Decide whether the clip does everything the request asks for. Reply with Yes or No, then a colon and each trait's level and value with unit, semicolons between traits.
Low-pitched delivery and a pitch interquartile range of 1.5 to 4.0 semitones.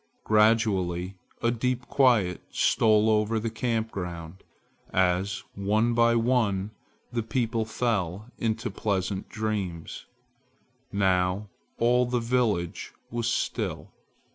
Yes: low, 110 Hz; average, 3.6 semitones